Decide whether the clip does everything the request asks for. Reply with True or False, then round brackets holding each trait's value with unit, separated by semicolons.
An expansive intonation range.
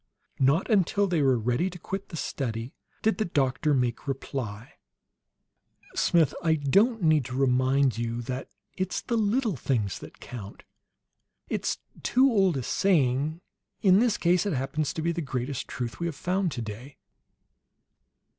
True (6.5 semitones)